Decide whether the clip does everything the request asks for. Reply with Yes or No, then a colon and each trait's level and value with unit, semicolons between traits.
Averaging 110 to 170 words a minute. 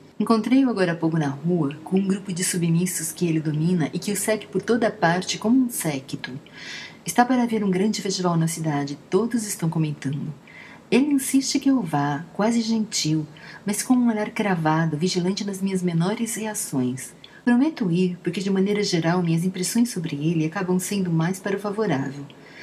No: average, 180 wpm